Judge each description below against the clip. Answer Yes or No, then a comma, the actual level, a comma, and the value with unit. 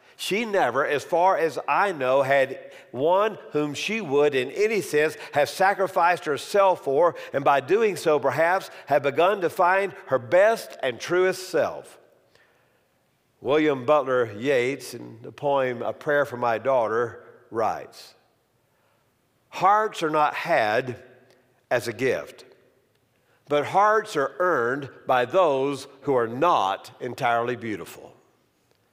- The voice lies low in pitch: No, medium, 150 Hz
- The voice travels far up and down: Yes, wide, 6.4 semitones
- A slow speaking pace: Yes, slow, 130 wpm